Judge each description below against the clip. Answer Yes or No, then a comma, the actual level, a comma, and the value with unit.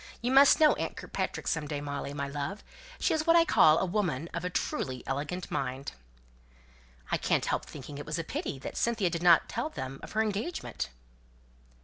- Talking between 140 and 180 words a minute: No, average, 200 wpm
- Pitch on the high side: No, medium, 170 Hz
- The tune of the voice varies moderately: No, wide, 7.2 semitones